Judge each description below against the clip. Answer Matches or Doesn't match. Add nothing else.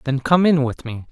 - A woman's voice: Doesn't match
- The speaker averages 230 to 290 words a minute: Matches